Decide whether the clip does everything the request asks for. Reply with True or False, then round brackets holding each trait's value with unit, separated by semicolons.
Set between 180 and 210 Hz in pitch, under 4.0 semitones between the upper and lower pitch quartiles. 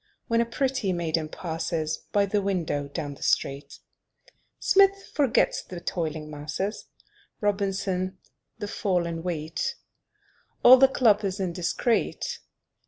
False (185 Hz; 4.4 semitones)